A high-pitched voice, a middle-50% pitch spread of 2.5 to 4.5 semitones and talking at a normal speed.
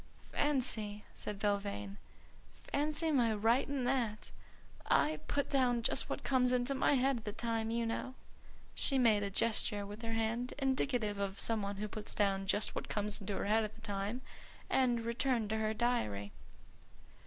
Yes: high, 225 Hz; average, 3.4 semitones; average, 170 wpm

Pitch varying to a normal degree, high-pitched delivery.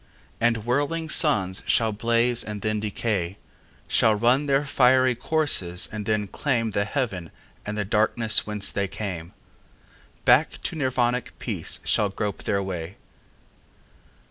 No: average, 3.7 semitones; low, 110 Hz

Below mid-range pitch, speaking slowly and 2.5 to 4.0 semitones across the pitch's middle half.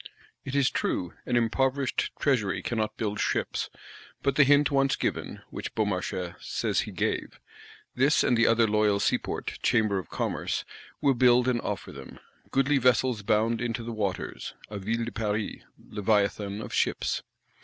No: low, 115 Hz; average, 155 wpm; average, 3.7 semitones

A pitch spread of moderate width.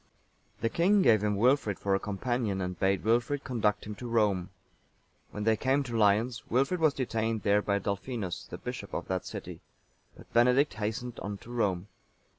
Yes: average, 3.5 semitones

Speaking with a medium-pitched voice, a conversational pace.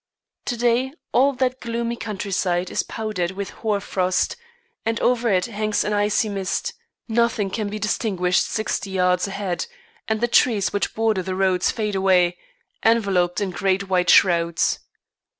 No: high, 200 Hz; average, 150 wpm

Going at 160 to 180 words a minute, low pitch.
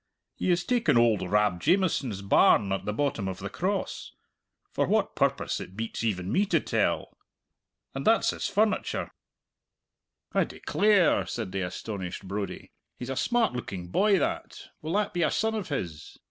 Yes: average, 170 wpm; low, 120 Hz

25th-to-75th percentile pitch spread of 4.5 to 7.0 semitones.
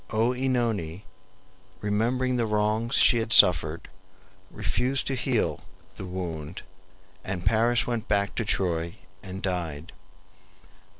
Yes: average, 5.0 semitones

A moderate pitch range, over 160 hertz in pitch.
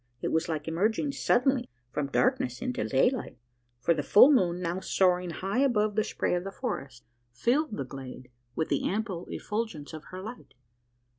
No: wide, 7.0 semitones; high, 190 Hz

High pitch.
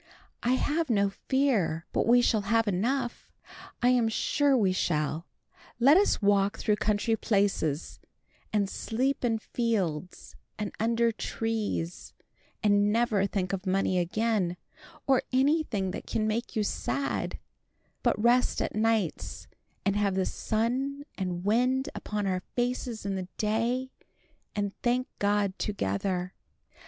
Yes: high, 215 Hz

